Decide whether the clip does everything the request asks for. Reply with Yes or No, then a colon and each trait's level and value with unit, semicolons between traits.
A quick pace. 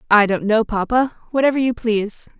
No: average, 175 wpm